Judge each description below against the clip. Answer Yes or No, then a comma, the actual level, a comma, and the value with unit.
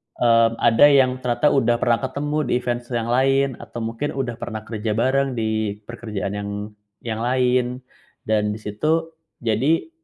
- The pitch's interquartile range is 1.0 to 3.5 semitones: Yes, average, 2.9 semitones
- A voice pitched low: Yes, low, 120 Hz